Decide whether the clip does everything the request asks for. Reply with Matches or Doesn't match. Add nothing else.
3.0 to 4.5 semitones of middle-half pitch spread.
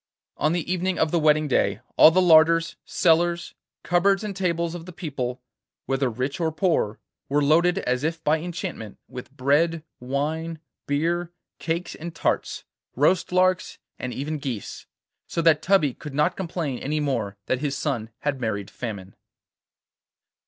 Matches